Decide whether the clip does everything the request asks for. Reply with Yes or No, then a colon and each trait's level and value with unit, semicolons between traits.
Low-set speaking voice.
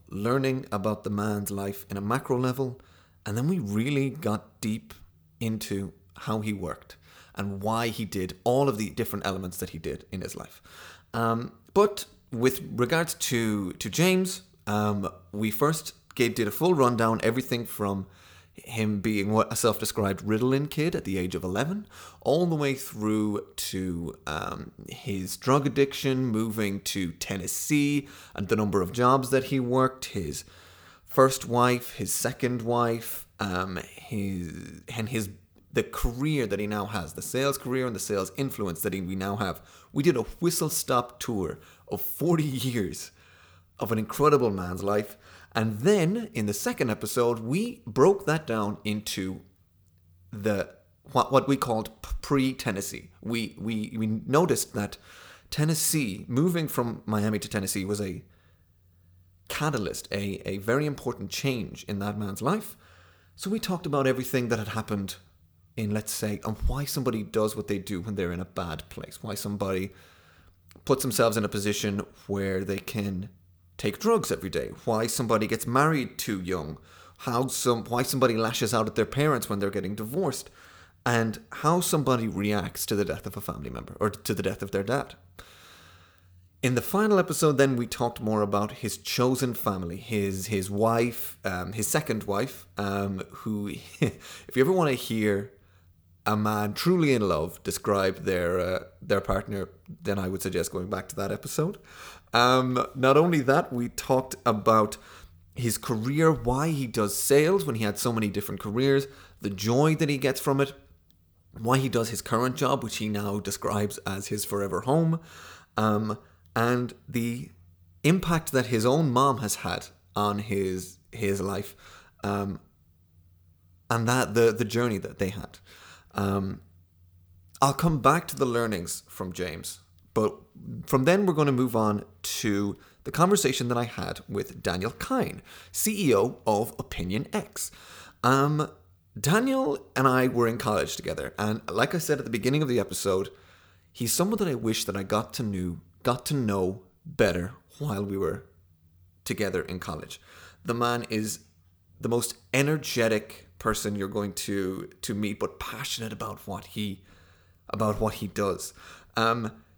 Yes: low, 105 Hz